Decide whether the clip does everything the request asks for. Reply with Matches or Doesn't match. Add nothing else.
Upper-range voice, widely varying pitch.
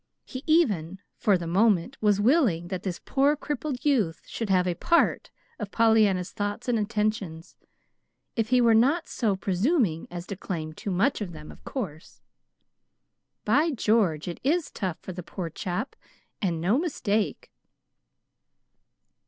Matches